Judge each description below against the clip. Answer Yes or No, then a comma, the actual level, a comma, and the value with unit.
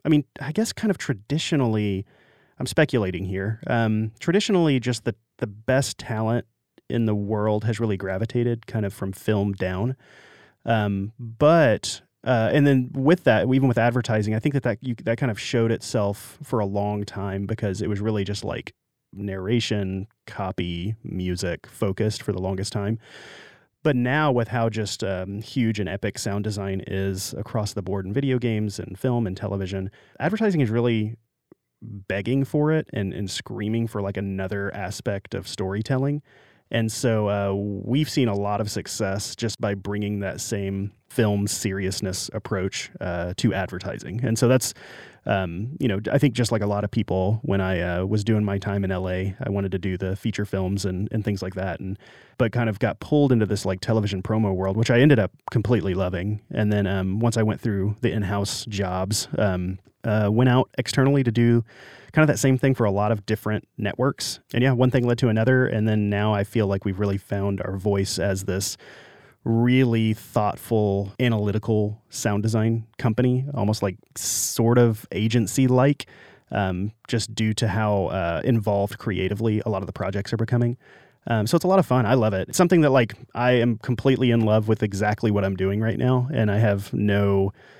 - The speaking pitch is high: No, low, 110 Hz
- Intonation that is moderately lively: Yes, average, 3.3 semitones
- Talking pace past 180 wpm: Yes, average, 190 wpm